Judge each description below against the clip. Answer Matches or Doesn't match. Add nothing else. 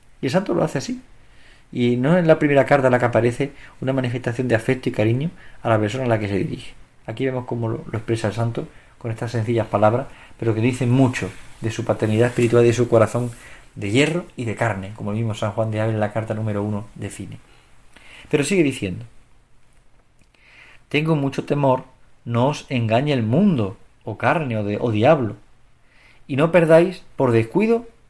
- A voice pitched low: Matches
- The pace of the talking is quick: Matches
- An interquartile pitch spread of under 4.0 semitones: Matches